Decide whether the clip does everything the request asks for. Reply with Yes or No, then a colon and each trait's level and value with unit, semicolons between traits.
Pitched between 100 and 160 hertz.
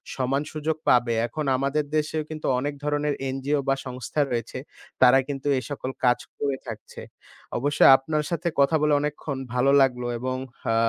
Yes: medium, 140 Hz